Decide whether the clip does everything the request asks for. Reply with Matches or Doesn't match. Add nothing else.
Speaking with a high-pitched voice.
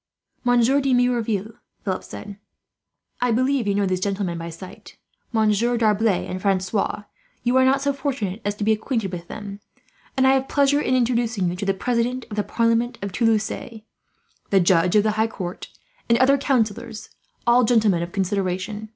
Matches